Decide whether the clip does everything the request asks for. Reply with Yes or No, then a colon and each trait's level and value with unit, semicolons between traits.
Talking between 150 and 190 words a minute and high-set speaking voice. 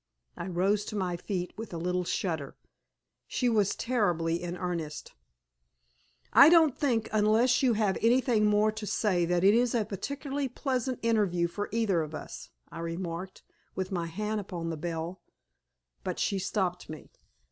Yes: average, 160 wpm; high, 195 Hz